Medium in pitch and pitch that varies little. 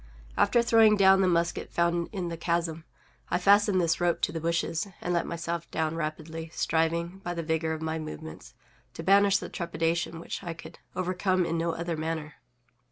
Yes: medium, 170 Hz; narrow, 1.9 semitones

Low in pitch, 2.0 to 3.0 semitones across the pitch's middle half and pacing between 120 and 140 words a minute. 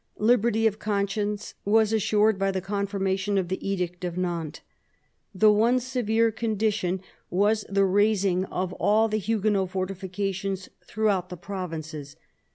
No: high, 200 Hz; narrow, 2.5 semitones; slow, 135 wpm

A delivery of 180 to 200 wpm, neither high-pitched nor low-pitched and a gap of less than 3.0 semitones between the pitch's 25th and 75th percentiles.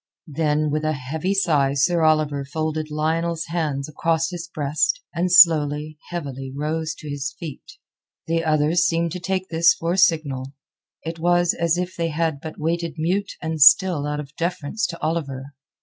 No: average, 170 wpm; medium, 160 Hz; narrow, 2.4 semitones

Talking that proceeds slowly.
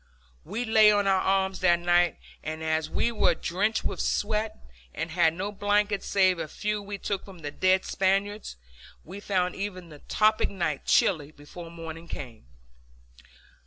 No: average, 160 wpm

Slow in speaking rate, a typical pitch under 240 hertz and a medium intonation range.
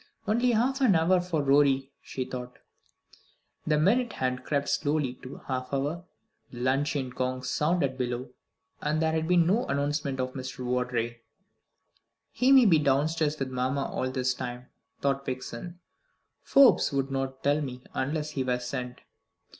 No: average, 155 wpm; medium, 140 Hz; average, 3.8 semitones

